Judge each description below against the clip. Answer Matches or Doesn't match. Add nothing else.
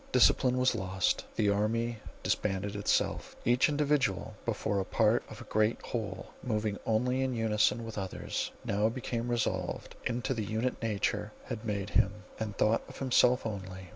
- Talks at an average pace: Matches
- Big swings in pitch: Doesn't match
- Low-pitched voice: Matches